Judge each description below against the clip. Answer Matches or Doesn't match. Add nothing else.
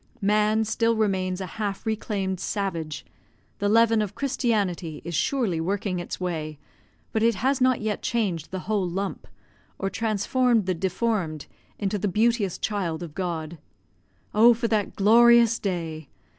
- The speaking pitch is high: Matches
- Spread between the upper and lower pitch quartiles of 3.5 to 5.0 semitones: Matches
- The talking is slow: Doesn't match